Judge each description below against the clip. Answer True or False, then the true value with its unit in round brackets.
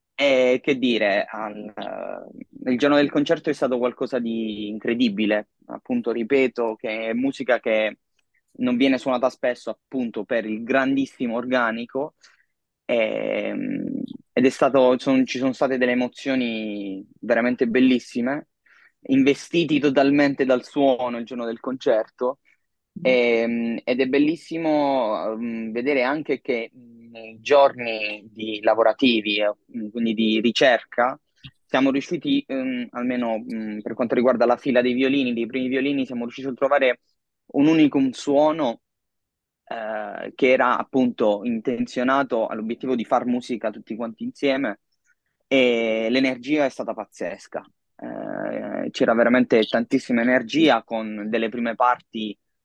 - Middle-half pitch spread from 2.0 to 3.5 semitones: True (2.9 semitones)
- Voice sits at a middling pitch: False (125 Hz)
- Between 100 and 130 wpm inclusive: True (120 wpm)